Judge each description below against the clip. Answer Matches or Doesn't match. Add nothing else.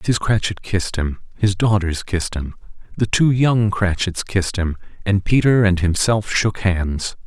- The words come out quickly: Doesn't match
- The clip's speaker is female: Doesn't match